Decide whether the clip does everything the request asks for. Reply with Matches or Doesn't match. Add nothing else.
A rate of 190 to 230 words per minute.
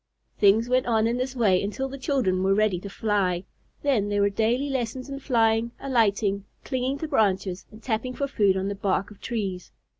Matches